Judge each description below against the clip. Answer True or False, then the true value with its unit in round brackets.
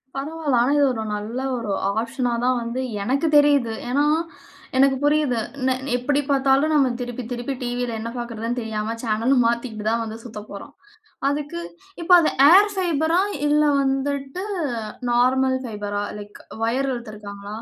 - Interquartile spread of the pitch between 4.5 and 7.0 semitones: False (3.7 semitones)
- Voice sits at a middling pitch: False (250 Hz)